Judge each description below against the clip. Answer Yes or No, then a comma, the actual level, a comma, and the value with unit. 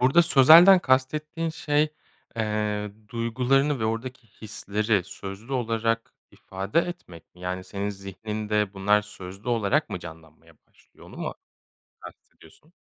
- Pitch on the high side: No, low, 110 Hz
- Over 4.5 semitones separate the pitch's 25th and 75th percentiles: Yes, average, 5.1 semitones